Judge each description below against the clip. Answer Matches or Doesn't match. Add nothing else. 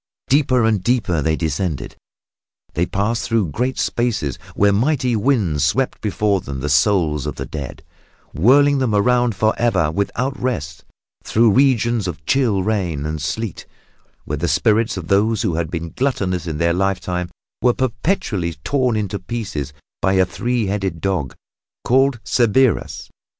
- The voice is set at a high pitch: Doesn't match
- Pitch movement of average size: Doesn't match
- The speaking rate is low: Doesn't match